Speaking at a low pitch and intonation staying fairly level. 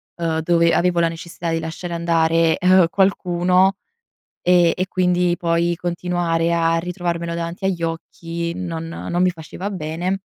No: medium, 170 Hz; narrow, 1.3 semitones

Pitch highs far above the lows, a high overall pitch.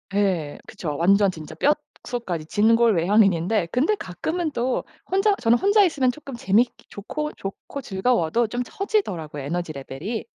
Yes: wide, 6.5 semitones; high, 215 Hz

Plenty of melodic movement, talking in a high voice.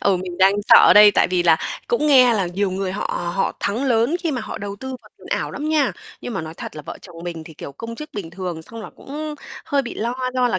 Yes: wide, 6.1 semitones; high, 205 Hz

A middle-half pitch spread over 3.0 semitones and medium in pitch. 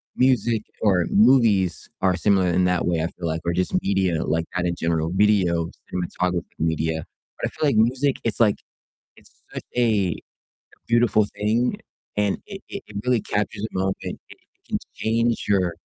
No: average, 4.5 semitones; very low, 95 Hz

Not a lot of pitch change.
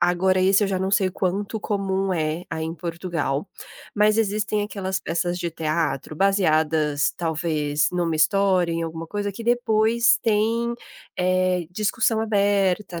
No: average, 3.8 semitones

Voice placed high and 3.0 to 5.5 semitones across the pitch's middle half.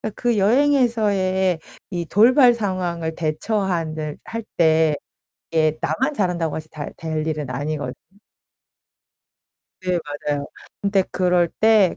No: medium, 180 Hz; average, 5.1 semitones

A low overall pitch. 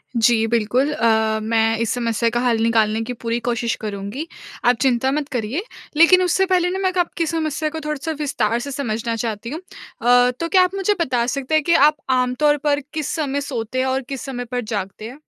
No: very high, 250 Hz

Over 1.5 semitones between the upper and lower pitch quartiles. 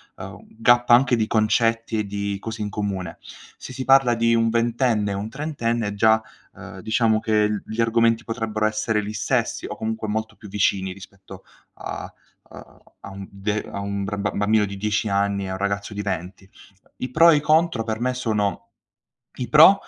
Yes: narrow, 2.4 semitones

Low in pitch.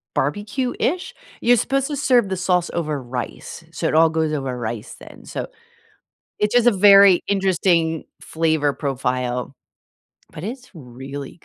No: medium, 165 Hz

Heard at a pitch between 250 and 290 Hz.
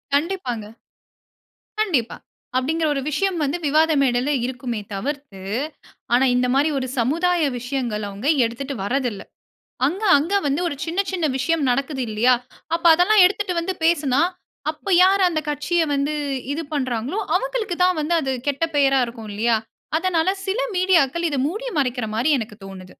Yes: very high, 285 Hz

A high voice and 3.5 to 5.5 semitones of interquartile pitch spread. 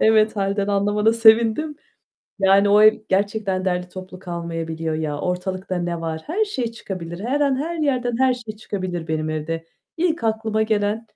Yes: high, 205 Hz; average, 4.1 semitones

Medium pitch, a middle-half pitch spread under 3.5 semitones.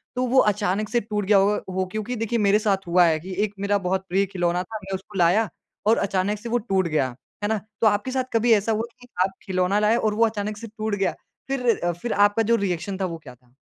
No: high, 205 Hz; average, 2.8 semitones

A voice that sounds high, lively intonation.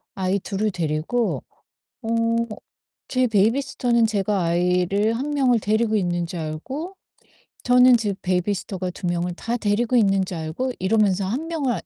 No: high, 210 Hz; average, 4.9 semitones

